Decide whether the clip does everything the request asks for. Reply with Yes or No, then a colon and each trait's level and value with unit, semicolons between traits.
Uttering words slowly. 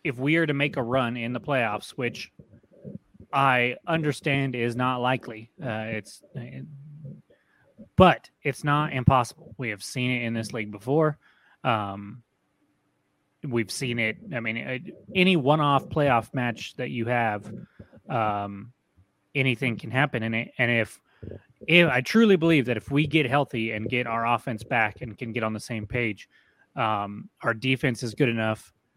No: average, 165 wpm